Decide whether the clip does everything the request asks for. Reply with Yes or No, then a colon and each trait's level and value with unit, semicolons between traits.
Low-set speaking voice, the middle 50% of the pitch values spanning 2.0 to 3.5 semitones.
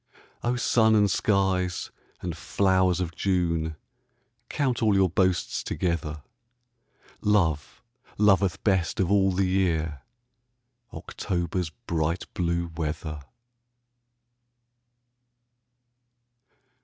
Yes: very low, 90 Hz; average, 2.8 semitones